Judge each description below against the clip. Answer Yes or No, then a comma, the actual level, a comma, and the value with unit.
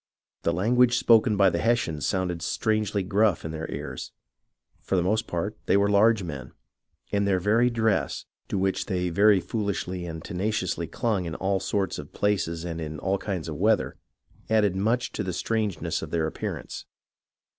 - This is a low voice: Yes, low, 100 Hz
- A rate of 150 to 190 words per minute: Yes, average, 175 wpm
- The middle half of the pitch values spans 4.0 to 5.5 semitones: No, average, 3.6 semitones